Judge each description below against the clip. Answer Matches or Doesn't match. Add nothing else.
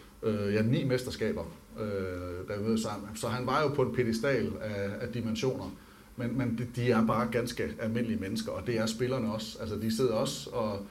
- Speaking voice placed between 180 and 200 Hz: Doesn't match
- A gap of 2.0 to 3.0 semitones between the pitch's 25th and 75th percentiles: Matches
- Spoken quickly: Doesn't match